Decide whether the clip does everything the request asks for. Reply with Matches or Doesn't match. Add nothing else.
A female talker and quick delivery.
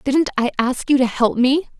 Matches